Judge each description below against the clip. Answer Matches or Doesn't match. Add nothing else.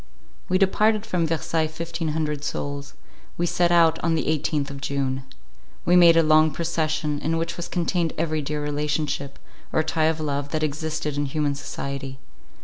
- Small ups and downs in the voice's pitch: Matches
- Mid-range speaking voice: Matches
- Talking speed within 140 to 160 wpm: Doesn't match